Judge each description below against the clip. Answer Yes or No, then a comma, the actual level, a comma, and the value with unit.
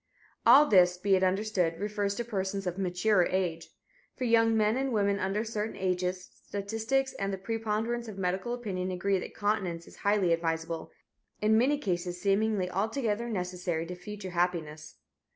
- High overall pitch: Yes, high, 195 Hz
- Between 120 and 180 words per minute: Yes, average, 160 wpm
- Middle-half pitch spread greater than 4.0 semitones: No, average, 3.4 semitones